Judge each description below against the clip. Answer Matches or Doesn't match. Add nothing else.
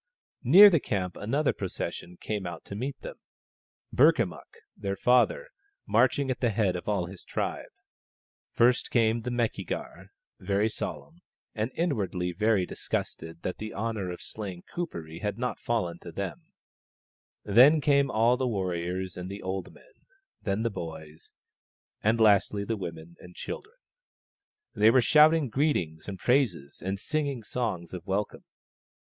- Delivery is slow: Doesn't match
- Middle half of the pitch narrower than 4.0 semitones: Doesn't match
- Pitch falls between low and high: Doesn't match